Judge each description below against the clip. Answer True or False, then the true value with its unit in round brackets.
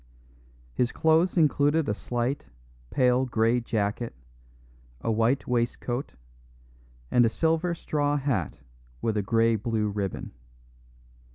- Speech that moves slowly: True (110 wpm)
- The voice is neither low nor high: False (120 Hz)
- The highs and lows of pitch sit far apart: False (4.3 semitones)